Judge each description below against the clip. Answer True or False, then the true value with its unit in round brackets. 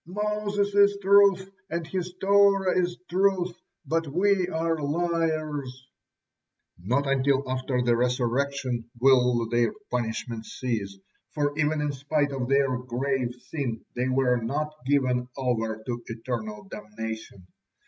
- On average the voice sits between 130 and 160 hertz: True (135 Hz)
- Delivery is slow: True (125 wpm)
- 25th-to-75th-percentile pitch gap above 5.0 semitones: True (5.6 semitones)